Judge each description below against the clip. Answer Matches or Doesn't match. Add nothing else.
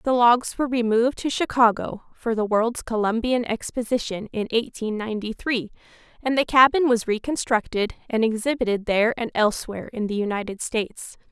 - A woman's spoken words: Matches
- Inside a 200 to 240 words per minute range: Doesn't match